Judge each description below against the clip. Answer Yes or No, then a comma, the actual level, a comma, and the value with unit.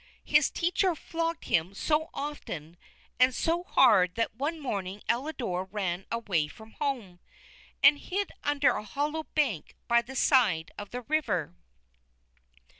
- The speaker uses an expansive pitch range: Yes, wide, 7.7 semitones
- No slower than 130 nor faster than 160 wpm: Yes, slow, 135 wpm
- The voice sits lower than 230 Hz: No, high, 245 Hz